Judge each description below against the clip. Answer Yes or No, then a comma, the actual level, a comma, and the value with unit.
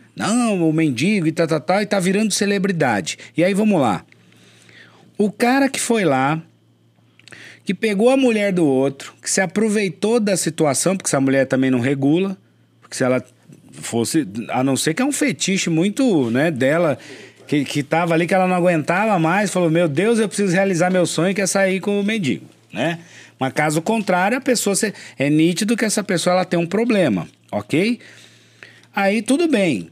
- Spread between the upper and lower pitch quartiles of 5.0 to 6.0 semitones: Yes, wide, 5.4 semitones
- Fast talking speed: Yes, fast, 190 wpm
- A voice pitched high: No, medium, 180 Hz